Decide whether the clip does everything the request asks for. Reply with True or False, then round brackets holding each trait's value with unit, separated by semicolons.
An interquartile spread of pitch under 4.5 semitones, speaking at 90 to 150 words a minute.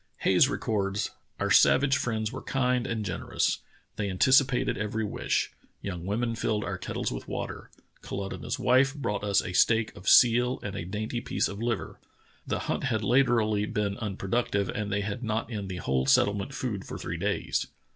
False (3.4 semitones; 175 wpm)